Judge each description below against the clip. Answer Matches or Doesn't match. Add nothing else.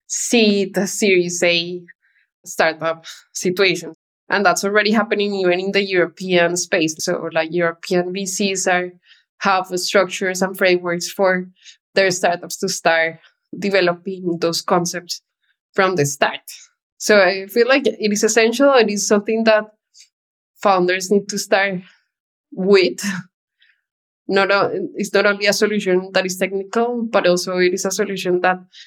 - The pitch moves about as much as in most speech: Doesn't match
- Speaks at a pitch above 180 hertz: Matches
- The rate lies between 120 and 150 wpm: Matches